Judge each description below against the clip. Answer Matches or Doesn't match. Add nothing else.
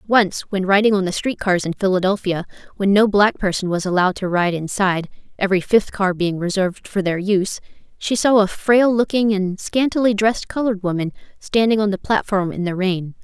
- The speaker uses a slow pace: Doesn't match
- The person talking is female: Matches